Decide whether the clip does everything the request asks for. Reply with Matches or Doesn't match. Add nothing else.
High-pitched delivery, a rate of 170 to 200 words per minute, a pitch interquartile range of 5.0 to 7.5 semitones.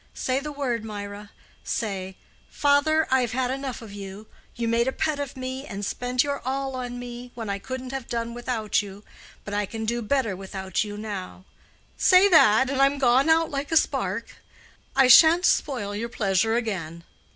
Doesn't match